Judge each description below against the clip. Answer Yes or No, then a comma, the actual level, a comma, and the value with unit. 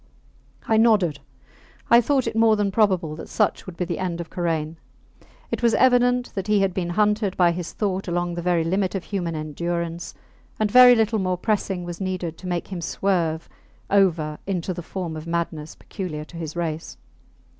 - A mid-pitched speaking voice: Yes, medium, 180 Hz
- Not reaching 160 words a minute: No, average, 190 wpm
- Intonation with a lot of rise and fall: No, average, 3.5 semitones